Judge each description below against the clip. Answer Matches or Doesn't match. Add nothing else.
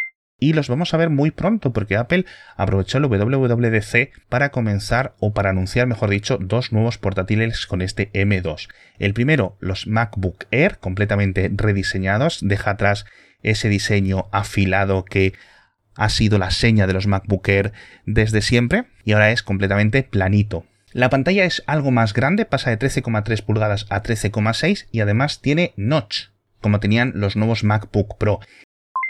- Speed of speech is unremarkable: Matches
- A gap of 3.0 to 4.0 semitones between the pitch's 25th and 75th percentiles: Matches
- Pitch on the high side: Doesn't match